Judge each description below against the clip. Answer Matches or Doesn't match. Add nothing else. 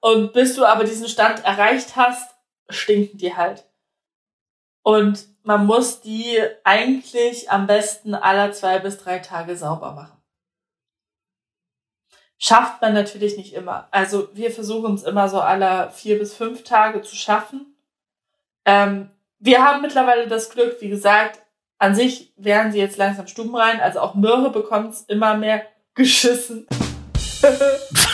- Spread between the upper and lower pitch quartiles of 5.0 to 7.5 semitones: Doesn't match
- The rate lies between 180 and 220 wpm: Doesn't match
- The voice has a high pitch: Matches